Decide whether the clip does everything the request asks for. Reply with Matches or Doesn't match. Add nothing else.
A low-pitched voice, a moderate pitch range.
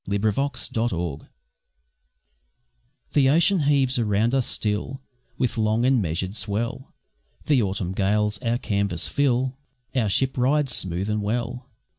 Matches